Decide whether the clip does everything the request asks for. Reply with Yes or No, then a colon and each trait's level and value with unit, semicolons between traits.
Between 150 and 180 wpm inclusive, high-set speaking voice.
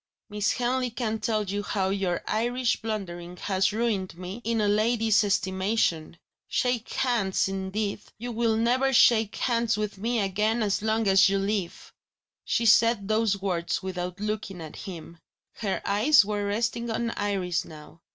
Yes: average, 155 wpm; high, 210 Hz